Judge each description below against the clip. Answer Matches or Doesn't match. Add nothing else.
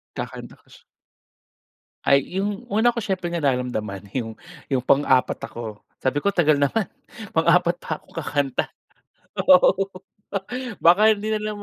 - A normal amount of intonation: Doesn't match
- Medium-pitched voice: Matches